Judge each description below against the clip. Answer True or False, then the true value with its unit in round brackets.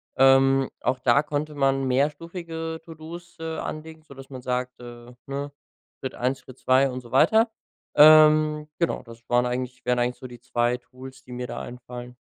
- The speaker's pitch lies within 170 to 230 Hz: False (135 Hz)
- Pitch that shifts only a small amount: False (3.7 semitones)